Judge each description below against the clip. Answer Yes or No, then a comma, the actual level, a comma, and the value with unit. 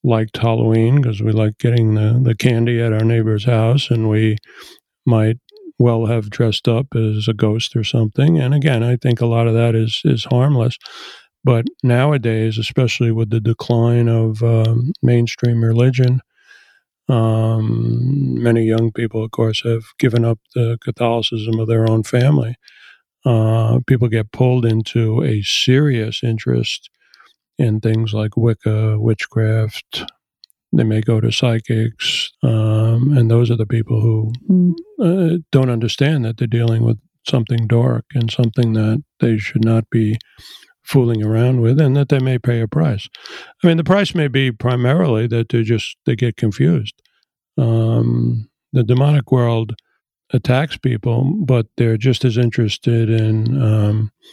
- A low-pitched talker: Yes, low, 115 Hz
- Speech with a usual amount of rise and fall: No, narrow, 2.1 semitones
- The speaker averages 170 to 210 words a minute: No, average, 150 wpm